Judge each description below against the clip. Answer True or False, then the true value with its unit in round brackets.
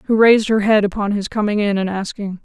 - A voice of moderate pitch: False (205 Hz)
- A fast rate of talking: True (245 wpm)